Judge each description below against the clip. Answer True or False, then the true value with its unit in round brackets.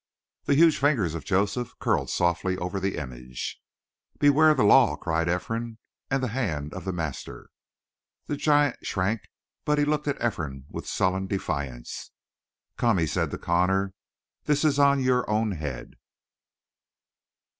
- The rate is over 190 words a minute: False (150 wpm)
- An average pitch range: False (7.8 semitones)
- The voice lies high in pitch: False (100 Hz)